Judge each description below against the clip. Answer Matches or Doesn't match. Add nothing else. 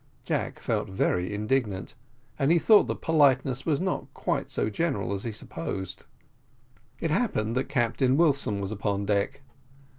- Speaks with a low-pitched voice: Matches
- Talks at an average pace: Matches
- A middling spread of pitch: Doesn't match